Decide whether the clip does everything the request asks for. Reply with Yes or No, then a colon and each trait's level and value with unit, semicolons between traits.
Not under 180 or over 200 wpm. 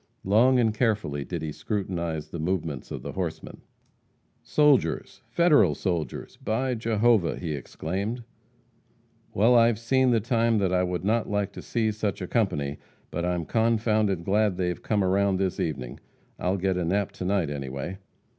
No: average, 160 wpm